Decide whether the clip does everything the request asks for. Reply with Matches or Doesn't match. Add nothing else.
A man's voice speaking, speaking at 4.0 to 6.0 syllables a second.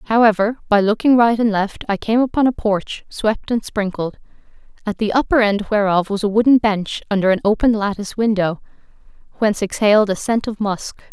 Doesn't match